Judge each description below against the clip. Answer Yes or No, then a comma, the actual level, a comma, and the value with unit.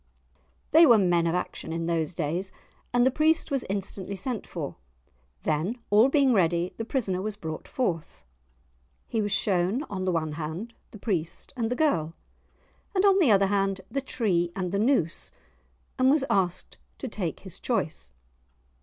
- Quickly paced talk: No, average, 170 wpm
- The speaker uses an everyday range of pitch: No, wide, 6.2 semitones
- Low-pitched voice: No, high, 195 Hz